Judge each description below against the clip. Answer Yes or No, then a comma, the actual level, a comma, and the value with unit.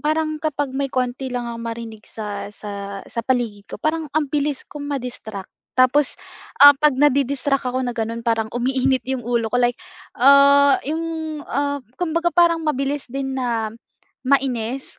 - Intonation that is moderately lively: Yes, average, 3.6 semitones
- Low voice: No, very high, 265 Hz